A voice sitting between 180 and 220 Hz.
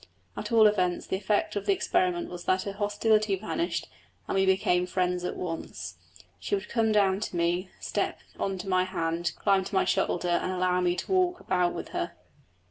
Yes: medium, 185 Hz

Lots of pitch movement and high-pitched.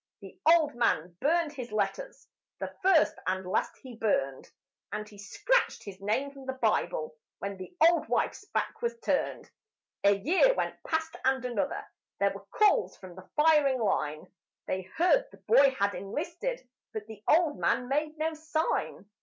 Yes: wide, 8.3 semitones; very high, 265 Hz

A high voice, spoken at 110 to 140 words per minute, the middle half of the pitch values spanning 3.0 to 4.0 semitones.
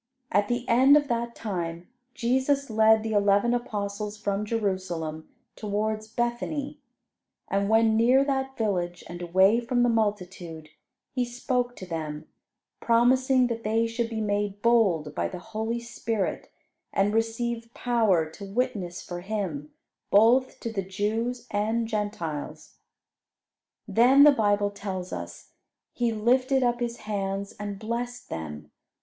Yes: high, 220 Hz; slow, 135 wpm; average, 3.4 semitones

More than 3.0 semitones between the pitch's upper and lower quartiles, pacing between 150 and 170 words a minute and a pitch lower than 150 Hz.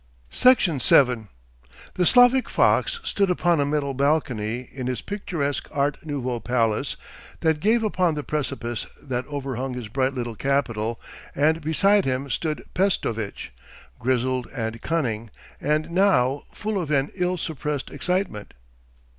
No: average, 5.2 semitones; slow, 135 wpm; medium, 140 Hz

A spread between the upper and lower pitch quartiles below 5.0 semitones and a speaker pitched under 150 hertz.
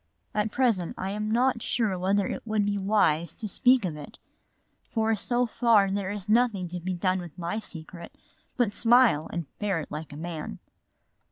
No: average, 4.1 semitones; high, 200 Hz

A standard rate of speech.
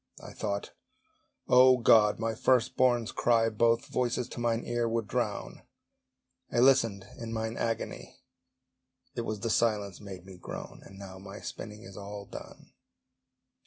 Yes: average, 150 wpm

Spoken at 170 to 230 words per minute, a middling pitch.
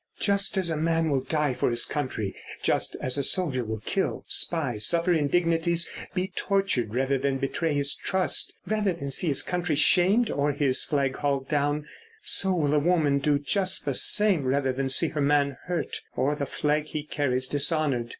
Yes: average, 185 wpm; medium, 145 Hz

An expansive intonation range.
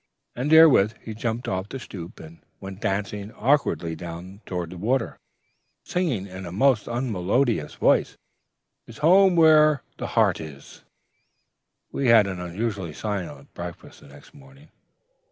Yes: wide, 6.9 semitones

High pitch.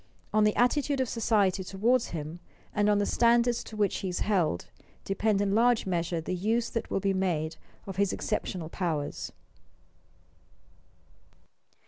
Yes: high, 200 Hz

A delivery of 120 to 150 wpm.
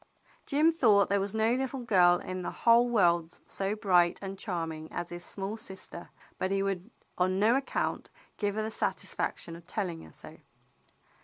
No: average, 175 wpm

